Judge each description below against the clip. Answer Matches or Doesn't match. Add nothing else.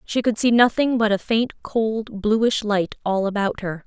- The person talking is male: Doesn't match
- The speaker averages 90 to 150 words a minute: Doesn't match